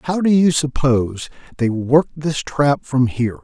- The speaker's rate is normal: Yes, average, 175 wpm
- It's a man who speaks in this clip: Yes, male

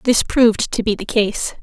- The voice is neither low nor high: No, high, 220 Hz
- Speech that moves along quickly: Yes, fast, 220 wpm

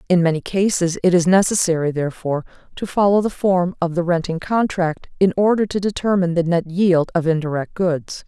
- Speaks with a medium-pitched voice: Yes, medium, 175 Hz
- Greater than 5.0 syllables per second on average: Yes, 5.6 syllables/s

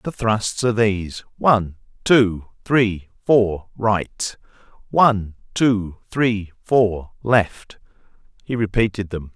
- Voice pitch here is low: Yes, low, 105 Hz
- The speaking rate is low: Yes, slow, 110 wpm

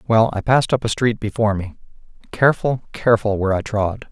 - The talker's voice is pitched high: No, low, 110 Hz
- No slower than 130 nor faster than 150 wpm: No, average, 190 wpm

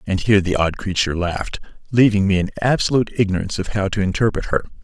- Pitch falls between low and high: No, low, 100 Hz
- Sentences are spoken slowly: No, average, 200 wpm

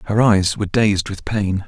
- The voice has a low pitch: Yes, low, 100 Hz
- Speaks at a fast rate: Yes, fast, 215 wpm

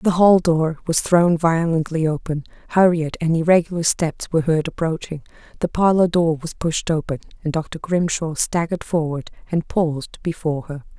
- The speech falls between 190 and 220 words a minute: No, average, 160 wpm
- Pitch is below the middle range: No, medium, 165 Hz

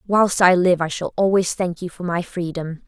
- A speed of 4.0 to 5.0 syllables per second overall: Yes, 4.8 syllables/s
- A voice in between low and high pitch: Yes, medium, 180 Hz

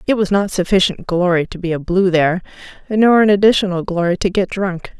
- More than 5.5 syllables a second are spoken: Yes, 5.7 syllables/s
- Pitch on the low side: No, medium, 185 Hz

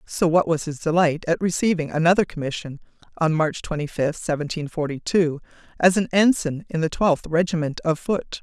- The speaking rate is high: No, average, 180 wpm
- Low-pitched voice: No, medium, 165 Hz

